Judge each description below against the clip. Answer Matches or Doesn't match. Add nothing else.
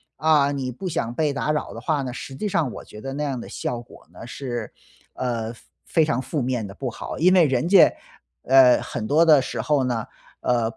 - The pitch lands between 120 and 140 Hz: Matches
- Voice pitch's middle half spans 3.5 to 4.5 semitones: Matches